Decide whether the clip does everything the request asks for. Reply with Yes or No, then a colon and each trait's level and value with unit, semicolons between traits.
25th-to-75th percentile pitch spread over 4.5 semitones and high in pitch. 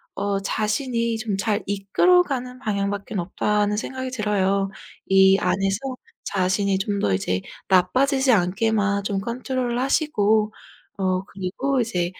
No: average, 4.0 semitones; high, 205 Hz